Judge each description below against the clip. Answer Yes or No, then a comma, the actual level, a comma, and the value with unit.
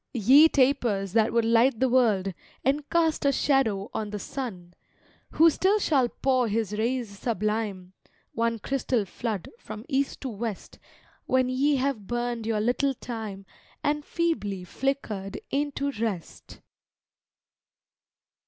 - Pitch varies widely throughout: No, average, 4.5 semitones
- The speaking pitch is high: Yes, high, 235 Hz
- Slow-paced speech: Yes, slow, 130 wpm